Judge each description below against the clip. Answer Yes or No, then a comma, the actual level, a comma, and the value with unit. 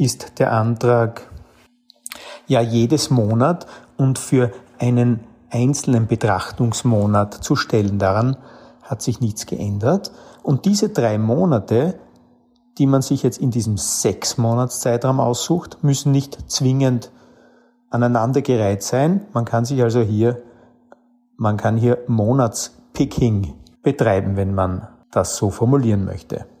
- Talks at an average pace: No, slow, 115 wpm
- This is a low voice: Yes, low, 120 Hz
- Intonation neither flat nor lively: Yes, average, 3.2 semitones